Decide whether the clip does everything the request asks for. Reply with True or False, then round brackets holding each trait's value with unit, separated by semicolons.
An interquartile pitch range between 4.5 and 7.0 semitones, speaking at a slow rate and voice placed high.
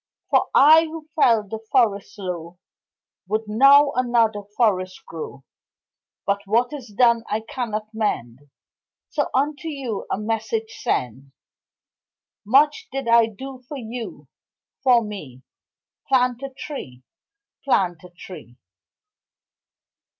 True (5.2 semitones; 115 wpm; 225 Hz)